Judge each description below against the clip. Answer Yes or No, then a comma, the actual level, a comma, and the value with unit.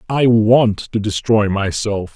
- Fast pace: No, average, 140 wpm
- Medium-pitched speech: No, low, 105 Hz